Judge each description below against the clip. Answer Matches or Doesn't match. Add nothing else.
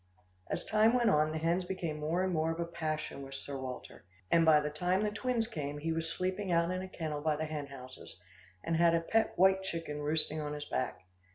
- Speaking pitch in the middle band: Matches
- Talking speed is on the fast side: Matches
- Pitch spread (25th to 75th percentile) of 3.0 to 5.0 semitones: Matches